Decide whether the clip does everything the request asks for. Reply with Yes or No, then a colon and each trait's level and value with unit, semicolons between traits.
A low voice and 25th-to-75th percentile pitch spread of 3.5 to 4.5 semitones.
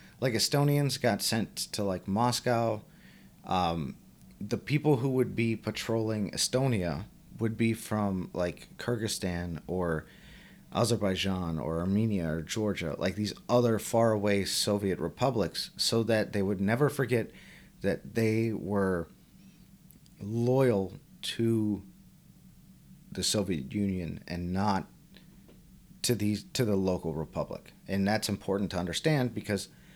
Yes: low, 105 Hz; average, 3.8 semitones